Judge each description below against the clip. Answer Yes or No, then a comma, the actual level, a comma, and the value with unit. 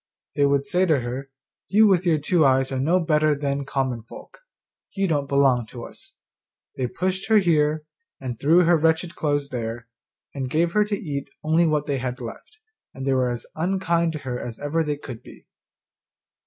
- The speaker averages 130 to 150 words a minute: No, average, 190 wpm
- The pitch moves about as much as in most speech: Yes, average, 4.1 semitones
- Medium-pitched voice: Yes, medium, 145 Hz